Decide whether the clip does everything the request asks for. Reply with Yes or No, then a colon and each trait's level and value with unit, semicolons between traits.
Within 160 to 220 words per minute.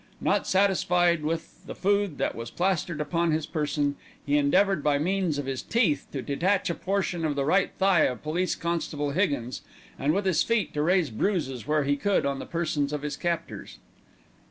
Yes: average, 190 wpm